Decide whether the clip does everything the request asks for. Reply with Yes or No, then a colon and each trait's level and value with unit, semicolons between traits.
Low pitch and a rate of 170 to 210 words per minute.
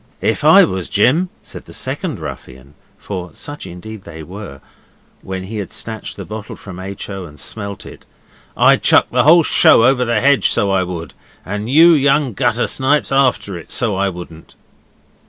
Yes: low, 105 Hz; average, 180 wpm